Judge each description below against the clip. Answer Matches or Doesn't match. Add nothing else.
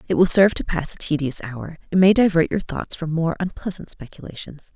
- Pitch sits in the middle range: Matches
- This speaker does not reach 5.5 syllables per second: Doesn't match